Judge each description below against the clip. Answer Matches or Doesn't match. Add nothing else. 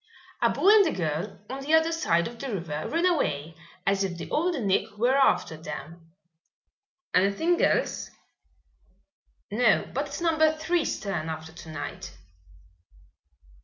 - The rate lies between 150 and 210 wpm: Doesn't match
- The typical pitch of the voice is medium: Doesn't match